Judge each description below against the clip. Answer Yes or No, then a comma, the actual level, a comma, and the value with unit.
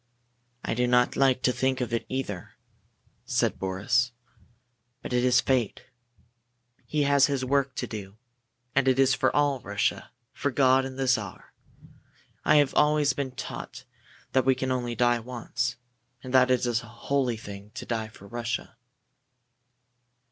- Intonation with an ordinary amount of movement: No, narrow, 2.1 semitones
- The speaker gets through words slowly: No, average, 160 wpm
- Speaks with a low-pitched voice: Yes, low, 125 Hz